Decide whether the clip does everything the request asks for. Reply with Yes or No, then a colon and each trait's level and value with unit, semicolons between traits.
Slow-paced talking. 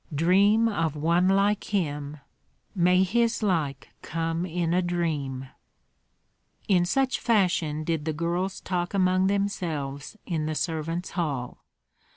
Yes: slow, 125 wpm